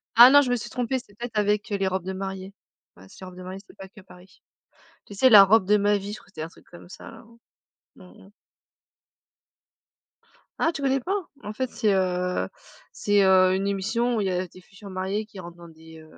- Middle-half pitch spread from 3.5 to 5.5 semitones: No, average, 2.8 semitones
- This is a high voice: Yes, high, 195 Hz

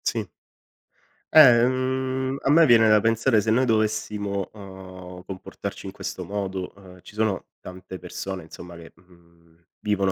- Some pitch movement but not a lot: Yes, average, 3.7 semitones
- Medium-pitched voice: No, low, 100 Hz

